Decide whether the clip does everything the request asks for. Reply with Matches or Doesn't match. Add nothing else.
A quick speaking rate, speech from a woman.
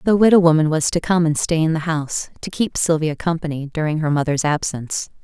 Matches